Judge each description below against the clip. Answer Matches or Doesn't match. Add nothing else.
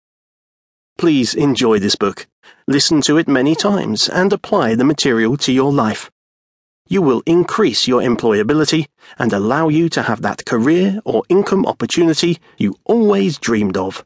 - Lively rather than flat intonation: Matches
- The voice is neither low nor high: Matches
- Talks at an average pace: Matches